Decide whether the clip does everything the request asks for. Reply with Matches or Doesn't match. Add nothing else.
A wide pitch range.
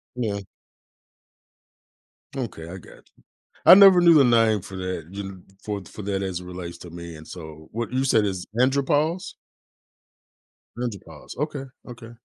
Matches